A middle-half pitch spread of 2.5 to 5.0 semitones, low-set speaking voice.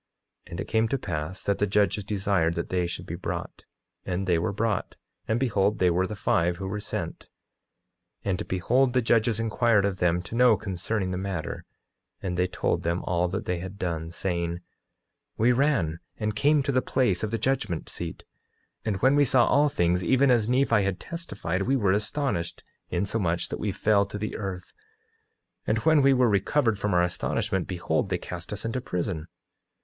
Yes: average, 4.5 semitones; low, 100 Hz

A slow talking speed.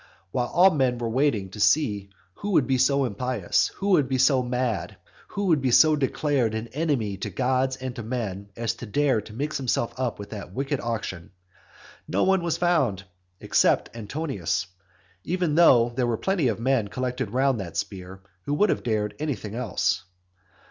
No: average, 185 wpm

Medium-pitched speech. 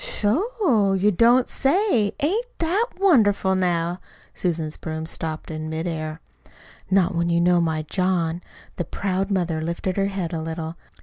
Yes: medium, 180 Hz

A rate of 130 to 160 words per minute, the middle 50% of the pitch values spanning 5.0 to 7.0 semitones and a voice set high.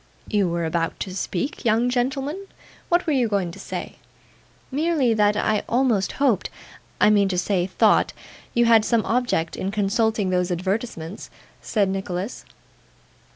No: average, 150 wpm; average, 4.6 semitones; high, 210 Hz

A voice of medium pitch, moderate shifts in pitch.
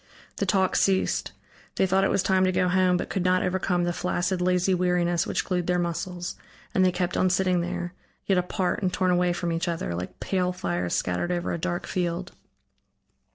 No: medium, 180 Hz; narrow, 1.0 semitones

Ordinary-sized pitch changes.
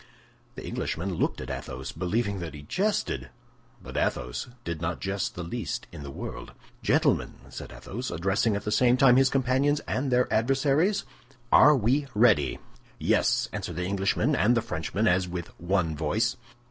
No: wide, 7.1 semitones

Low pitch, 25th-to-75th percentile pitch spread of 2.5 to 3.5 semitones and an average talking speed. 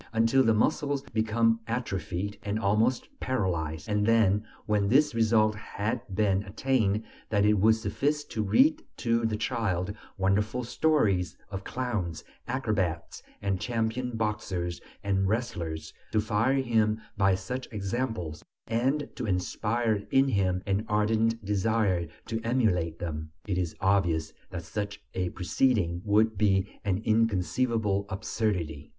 No: low, 105 Hz; average, 3.2 semitones; slow, 130 wpm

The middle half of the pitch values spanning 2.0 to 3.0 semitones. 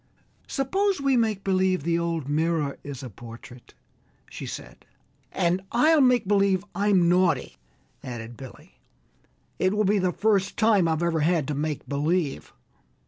No: wide, 5.5 semitones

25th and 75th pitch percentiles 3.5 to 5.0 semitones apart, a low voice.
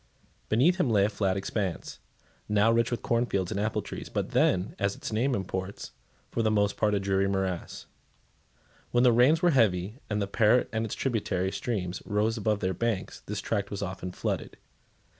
No: average, 3.0 semitones; low, 105 Hz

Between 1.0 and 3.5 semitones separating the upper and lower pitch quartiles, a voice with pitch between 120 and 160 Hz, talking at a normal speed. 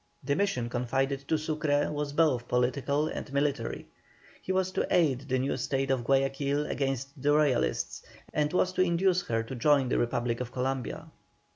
Yes: average, 2.8 semitones; medium, 140 Hz; average, 170 wpm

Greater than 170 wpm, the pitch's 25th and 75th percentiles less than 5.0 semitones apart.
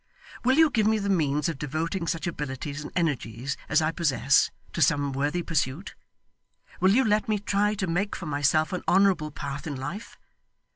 No: average, 185 wpm; wide, 5.5 semitones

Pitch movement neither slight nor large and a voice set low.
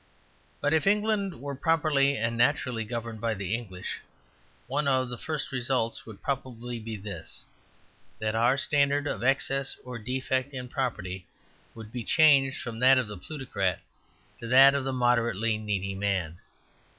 Yes: average, 3.9 semitones; low, 125 Hz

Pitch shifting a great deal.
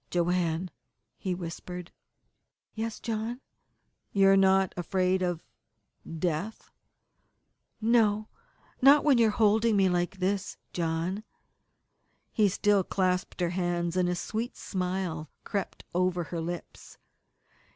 No: average, 3.0 semitones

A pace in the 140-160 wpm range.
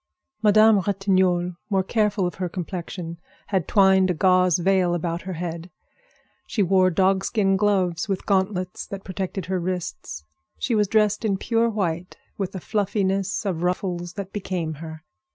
Yes: average, 155 wpm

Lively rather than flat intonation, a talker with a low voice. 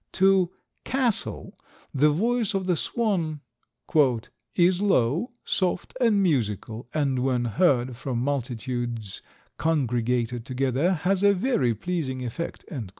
No: wide, 7.2 semitones; medium, 145 Hz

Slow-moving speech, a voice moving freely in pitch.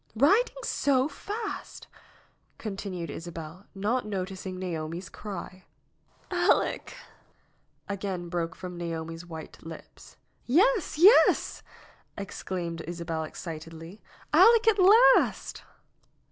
Yes: slow, 95 wpm; wide, 7.6 semitones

